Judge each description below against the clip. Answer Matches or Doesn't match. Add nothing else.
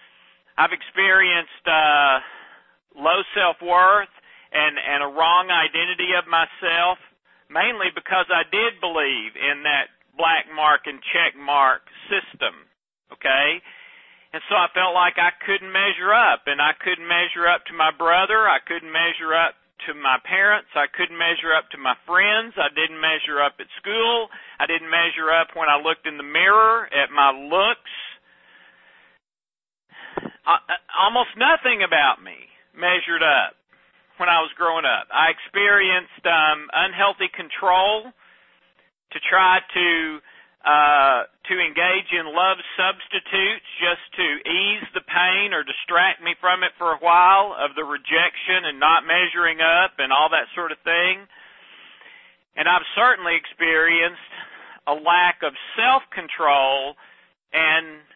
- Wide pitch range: Doesn't match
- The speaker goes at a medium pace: Matches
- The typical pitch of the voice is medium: Matches